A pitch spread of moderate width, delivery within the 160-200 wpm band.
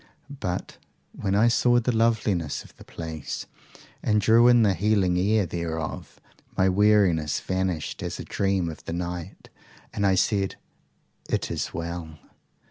No: average, 3.9 semitones; average, 145 wpm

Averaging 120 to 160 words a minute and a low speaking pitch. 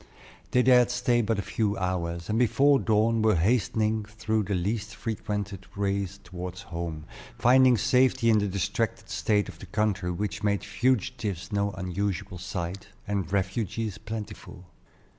Yes: average, 145 wpm; low, 105 Hz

